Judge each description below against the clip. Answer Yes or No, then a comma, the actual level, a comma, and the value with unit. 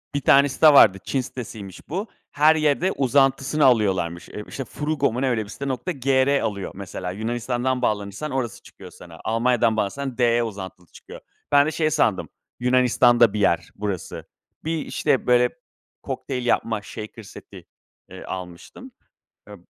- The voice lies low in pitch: Yes, low, 125 Hz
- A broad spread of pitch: No, average, 4.8 semitones